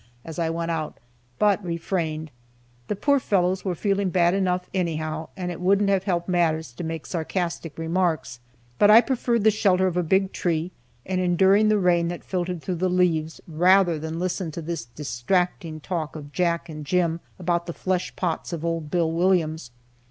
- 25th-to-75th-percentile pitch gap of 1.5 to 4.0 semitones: Yes, narrow, 2.5 semitones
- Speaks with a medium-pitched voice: Yes, medium, 175 Hz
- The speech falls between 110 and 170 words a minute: No, average, 180 wpm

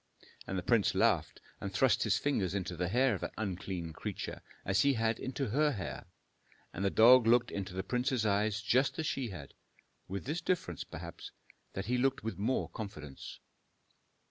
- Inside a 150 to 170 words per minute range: No, average, 180 wpm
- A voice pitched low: Yes, low, 110 Hz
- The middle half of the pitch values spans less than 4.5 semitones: No, average, 5.0 semitones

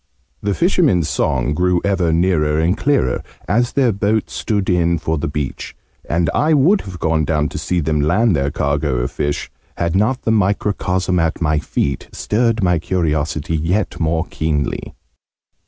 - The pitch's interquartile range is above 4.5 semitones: Yes, average, 4.9 semitones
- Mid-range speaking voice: No, very low, 85 Hz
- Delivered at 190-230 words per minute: No, average, 165 wpm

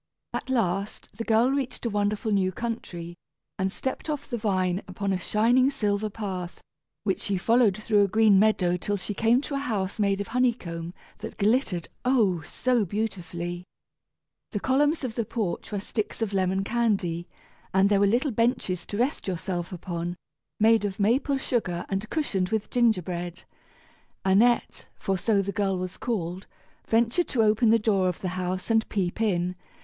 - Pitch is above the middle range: Yes, high, 205 Hz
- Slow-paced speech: No, average, 175 wpm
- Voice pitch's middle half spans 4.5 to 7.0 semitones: No, average, 3.8 semitones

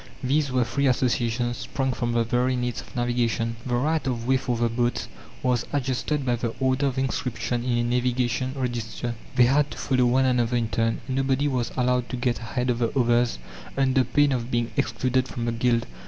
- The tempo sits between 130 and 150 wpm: No, average, 200 wpm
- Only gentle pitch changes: Yes, narrow, 1.6 semitones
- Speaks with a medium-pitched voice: No, low, 125 Hz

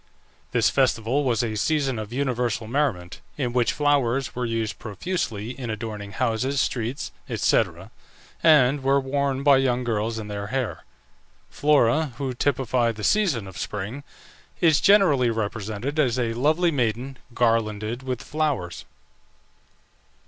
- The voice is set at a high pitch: No, low, 125 Hz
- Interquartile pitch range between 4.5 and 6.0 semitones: No, average, 3.9 semitones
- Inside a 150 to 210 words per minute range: No, slow, 135 wpm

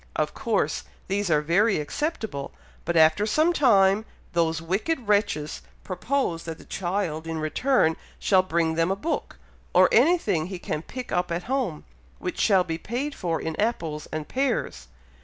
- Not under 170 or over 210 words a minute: No, average, 160 wpm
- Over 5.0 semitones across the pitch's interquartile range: Yes, wide, 5.5 semitones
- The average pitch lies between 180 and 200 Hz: Yes, medium, 185 Hz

